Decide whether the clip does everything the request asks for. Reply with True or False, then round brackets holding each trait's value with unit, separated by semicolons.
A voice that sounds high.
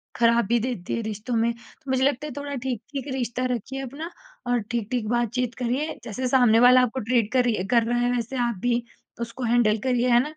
True (240 Hz)